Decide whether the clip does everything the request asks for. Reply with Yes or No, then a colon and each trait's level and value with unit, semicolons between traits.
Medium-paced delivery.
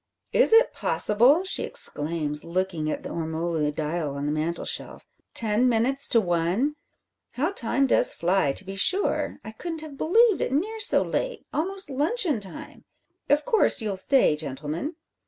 Yes: average, 155 wpm